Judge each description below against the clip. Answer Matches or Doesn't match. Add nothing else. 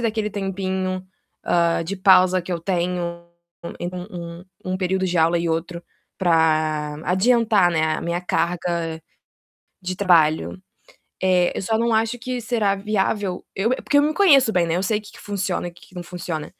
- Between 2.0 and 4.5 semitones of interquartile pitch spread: Matches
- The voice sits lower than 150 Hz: Doesn't match